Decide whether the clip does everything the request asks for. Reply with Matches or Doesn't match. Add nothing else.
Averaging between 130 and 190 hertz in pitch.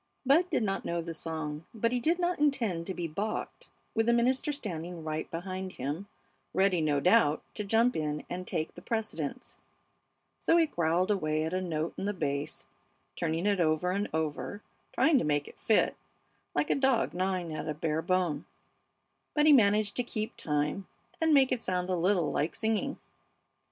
Matches